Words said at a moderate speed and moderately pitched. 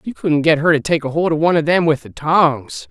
No: fast, 310 wpm; medium, 155 Hz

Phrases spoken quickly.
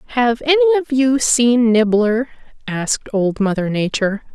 No: average, 140 wpm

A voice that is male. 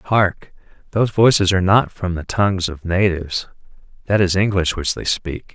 Yes: male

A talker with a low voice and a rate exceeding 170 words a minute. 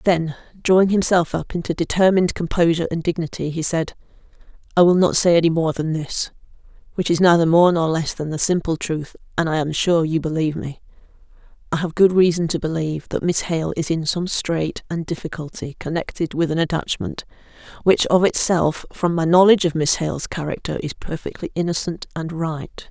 No: medium, 165 Hz; average, 180 wpm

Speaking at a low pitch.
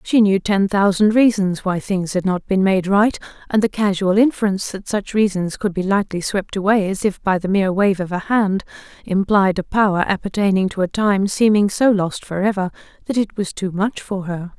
No: high, 195 Hz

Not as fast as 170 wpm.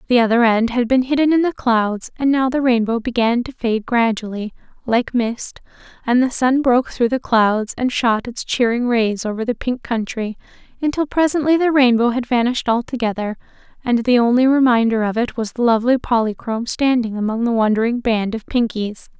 No: average, 185 wpm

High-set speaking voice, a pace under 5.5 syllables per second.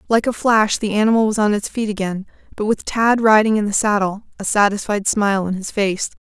No: high, 210 Hz; 5.6 syllables/s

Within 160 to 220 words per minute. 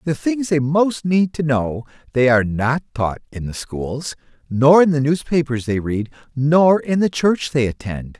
Yes: average, 190 wpm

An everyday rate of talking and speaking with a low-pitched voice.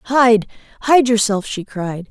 No: average, 145 wpm; high, 225 Hz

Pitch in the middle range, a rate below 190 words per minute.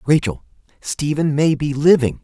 Yes: medium, 145 Hz; slow, 135 wpm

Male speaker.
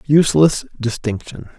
Yes: male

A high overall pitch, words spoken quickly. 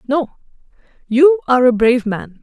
No: very high, 255 Hz; average, 150 wpm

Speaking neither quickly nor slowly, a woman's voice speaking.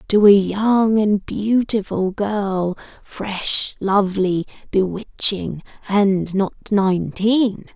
No: slow, 95 wpm; female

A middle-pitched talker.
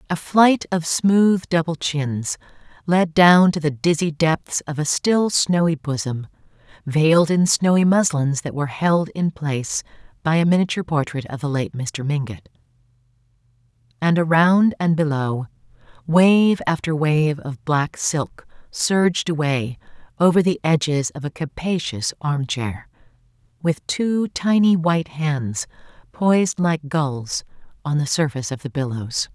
Yes: medium, 155 Hz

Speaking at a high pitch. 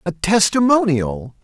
No: medium, 180 Hz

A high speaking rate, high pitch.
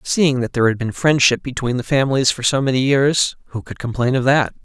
No: fast, 235 wpm; low, 130 Hz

